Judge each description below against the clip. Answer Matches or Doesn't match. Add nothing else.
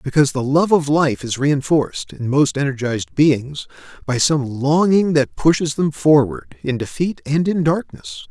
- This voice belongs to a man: Matches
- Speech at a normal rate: Matches